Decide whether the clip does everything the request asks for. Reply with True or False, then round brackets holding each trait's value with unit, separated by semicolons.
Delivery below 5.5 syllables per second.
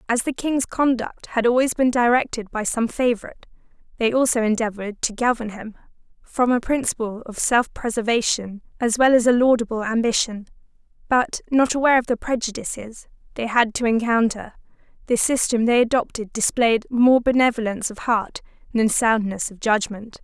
True (5.3 syllables/s)